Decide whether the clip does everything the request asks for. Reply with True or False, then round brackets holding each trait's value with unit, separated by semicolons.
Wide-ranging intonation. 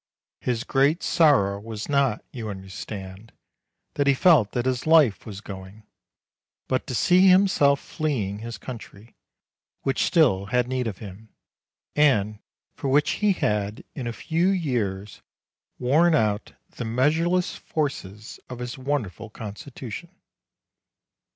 True (5.7 semitones)